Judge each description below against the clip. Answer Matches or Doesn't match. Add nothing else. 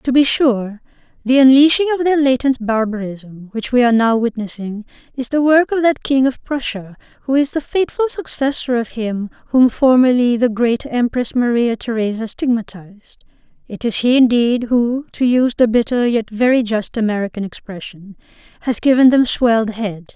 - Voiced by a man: Doesn't match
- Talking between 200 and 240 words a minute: Doesn't match